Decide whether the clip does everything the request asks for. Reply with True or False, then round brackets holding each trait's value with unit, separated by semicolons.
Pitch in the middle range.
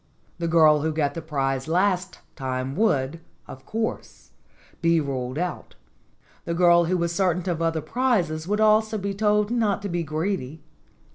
True (170 Hz)